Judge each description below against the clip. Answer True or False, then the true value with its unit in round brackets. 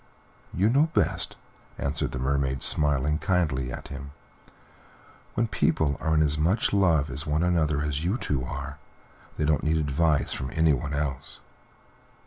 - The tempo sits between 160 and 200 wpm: False (150 wpm)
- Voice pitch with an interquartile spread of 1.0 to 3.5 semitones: True (2.7 semitones)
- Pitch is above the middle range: False (75 Hz)